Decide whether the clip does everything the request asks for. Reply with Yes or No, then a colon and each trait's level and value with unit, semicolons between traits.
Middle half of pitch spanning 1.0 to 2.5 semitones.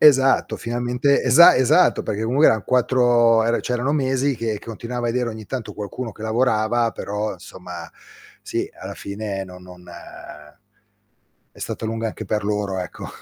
No: average, 2.9 semitones